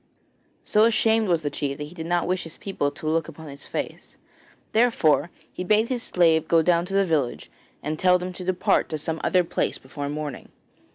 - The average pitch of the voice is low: No, medium, 165 Hz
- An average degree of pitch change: Yes, average, 3.3 semitones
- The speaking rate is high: Yes, fast, 210 wpm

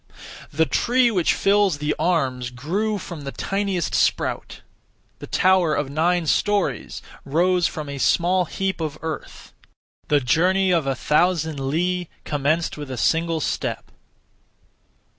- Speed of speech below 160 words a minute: Yes, slow, 135 wpm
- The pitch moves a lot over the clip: No, average, 3.9 semitones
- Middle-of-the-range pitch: Yes, medium, 165 Hz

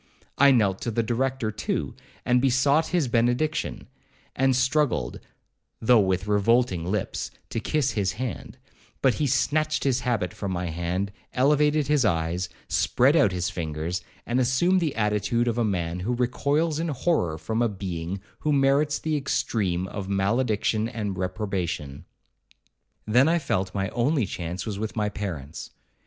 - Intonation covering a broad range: Yes, wide, 6.1 semitones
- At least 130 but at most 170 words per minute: Yes, average, 155 wpm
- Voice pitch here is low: Yes, low, 115 Hz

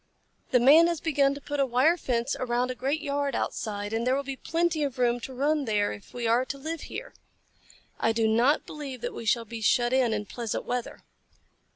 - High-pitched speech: Yes, very high, 255 Hz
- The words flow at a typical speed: No, fast, 220 wpm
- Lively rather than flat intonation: No, average, 3.6 semitones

